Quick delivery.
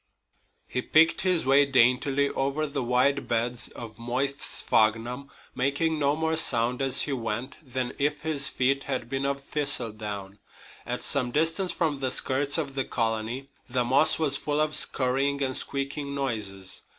No: average, 160 wpm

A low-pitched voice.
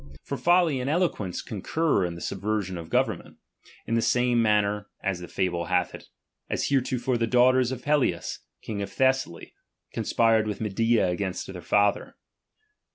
Yes: low, 110 Hz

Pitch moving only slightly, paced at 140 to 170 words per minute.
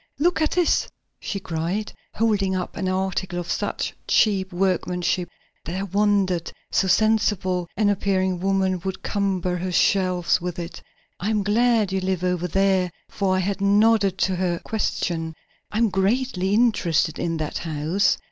Yes: narrow, 2.2 semitones; average, 155 wpm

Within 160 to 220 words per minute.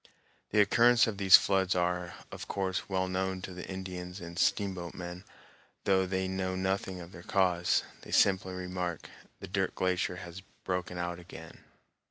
Yes: average, 165 wpm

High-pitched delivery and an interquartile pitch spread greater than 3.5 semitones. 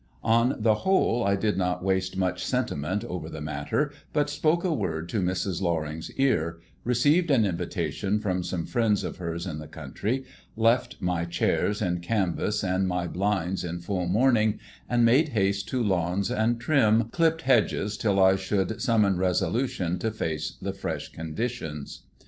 No: low, 100 Hz; average, 4.8 semitones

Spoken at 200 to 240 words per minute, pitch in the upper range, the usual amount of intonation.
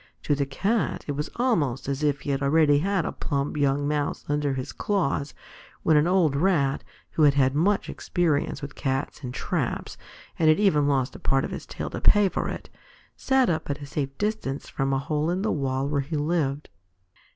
No: fast, 205 wpm; medium, 145 Hz; average, 3.3 semitones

